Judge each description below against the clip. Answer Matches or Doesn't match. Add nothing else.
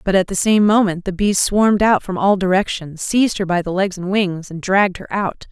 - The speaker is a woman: Matches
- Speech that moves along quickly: Matches